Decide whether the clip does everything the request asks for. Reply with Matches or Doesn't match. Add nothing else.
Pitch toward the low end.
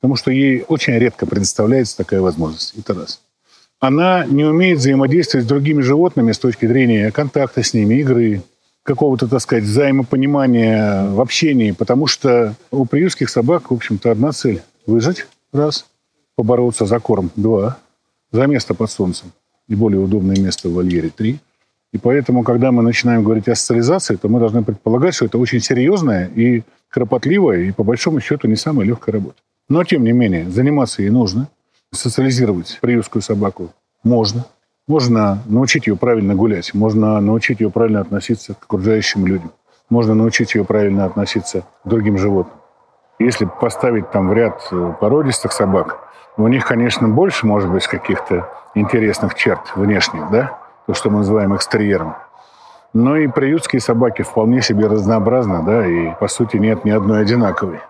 Matches